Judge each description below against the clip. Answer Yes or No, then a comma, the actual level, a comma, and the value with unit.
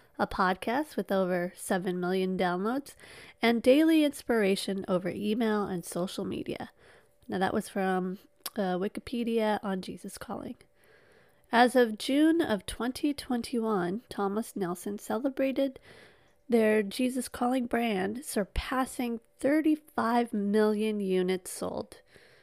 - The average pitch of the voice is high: Yes, high, 215 Hz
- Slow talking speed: Yes, slow, 110 wpm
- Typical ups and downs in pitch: Yes, average, 4.7 semitones